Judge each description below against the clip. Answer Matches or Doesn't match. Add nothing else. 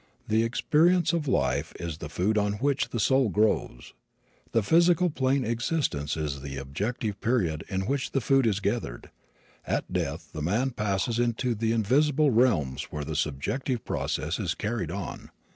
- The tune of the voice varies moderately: Doesn't match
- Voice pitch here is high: Doesn't match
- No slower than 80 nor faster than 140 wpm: Doesn't match